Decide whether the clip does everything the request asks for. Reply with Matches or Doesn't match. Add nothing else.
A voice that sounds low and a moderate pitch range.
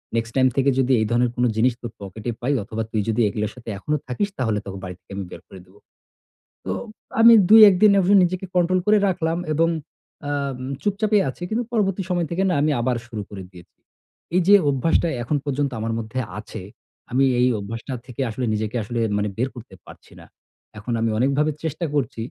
Doesn't match